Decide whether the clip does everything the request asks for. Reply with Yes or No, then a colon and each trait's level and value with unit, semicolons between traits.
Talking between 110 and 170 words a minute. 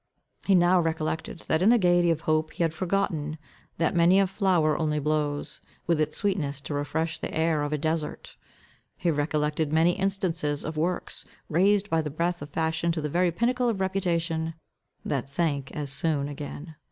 No: average, 180 wpm